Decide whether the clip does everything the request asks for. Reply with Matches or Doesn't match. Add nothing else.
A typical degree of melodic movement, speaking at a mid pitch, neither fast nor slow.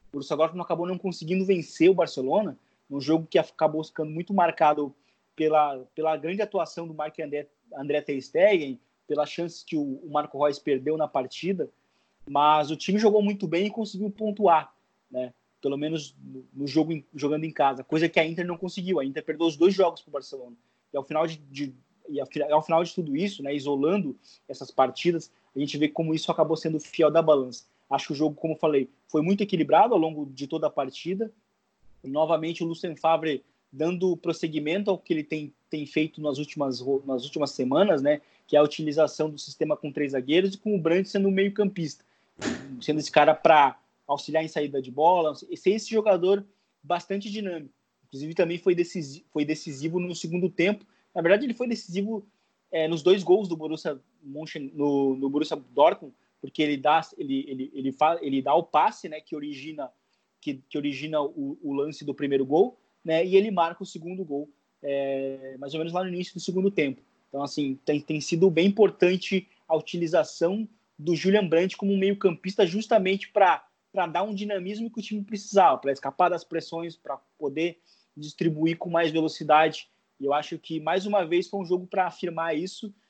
Doesn't match